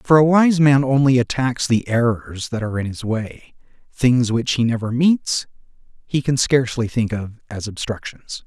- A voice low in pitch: Yes, low, 125 Hz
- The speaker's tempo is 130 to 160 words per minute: No, average, 175 wpm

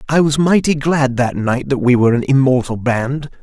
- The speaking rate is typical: No, fast, 210 wpm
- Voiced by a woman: No, male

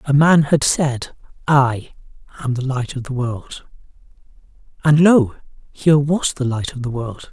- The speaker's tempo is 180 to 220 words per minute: No, average, 165 wpm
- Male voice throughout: Yes, male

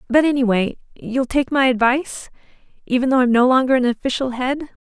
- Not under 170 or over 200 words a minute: Yes, average, 175 wpm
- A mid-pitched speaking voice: No, very high, 255 Hz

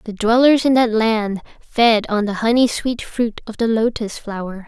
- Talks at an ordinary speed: Yes, average, 195 wpm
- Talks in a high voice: Yes, high, 225 Hz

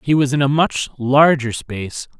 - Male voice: Yes, male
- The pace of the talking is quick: No, average, 190 wpm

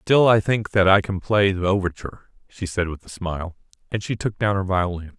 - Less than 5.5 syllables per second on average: No, 5.6 syllables/s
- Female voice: No, male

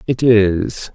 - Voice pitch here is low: Yes, low, 110 Hz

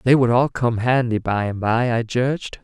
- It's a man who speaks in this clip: Yes, male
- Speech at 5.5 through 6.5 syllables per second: No, 4.8 syllables/s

